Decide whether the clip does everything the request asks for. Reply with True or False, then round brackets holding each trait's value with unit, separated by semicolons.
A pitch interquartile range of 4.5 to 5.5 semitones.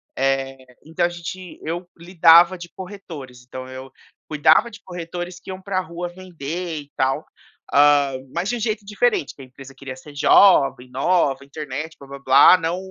True (4.8 semitones)